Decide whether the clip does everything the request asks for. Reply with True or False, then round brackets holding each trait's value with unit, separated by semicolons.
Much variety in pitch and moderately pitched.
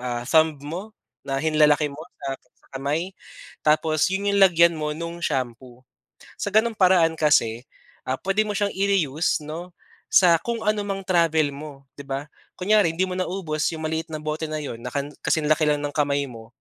False (4.1 semitones; 155 Hz)